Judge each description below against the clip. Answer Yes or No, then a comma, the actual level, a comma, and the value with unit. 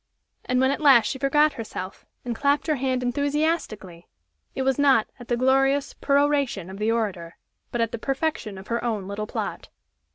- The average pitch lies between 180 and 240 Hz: No, very high, 250 Hz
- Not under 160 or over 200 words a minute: Yes, average, 185 wpm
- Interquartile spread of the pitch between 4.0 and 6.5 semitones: Yes, average, 4.6 semitones